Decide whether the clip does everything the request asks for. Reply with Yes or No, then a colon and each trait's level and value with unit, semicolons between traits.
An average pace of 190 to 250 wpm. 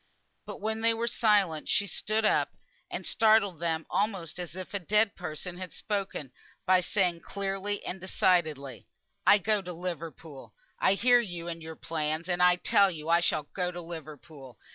No: average, 175 wpm